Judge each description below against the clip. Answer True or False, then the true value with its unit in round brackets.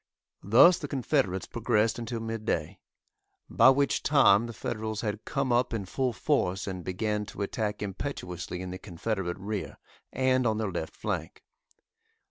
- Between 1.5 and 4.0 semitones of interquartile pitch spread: False (4.4 semitones)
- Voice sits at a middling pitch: False (110 Hz)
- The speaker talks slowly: False (155 wpm)